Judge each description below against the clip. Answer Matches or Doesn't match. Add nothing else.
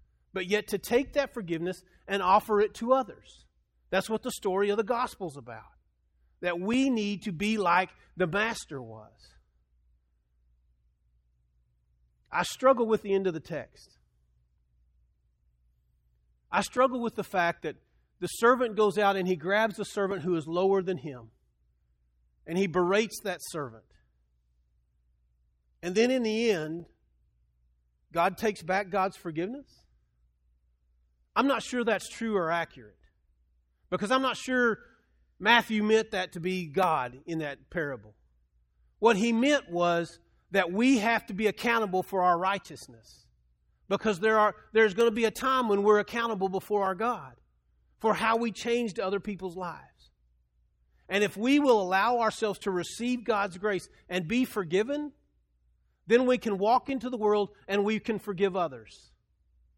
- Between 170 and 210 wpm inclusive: Doesn't match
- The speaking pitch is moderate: Matches